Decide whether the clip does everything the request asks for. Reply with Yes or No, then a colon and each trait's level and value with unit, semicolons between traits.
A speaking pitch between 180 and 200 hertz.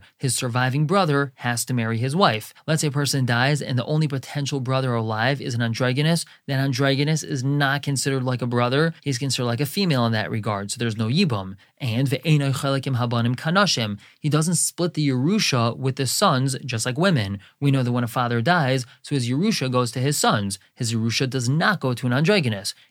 No: low, 135 Hz